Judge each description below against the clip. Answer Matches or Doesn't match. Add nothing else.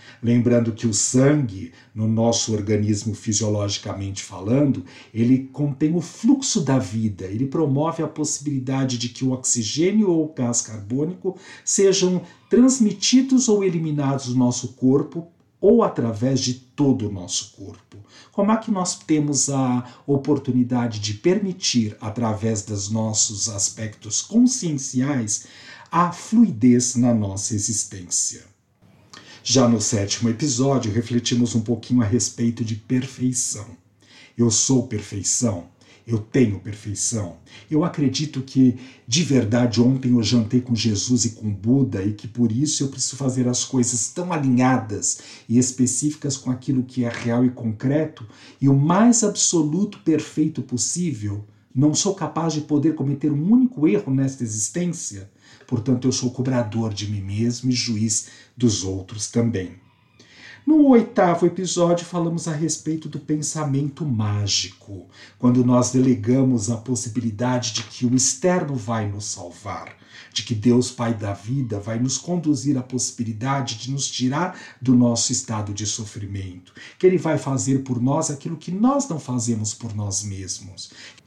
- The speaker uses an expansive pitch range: Doesn't match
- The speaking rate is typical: Matches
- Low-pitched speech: Matches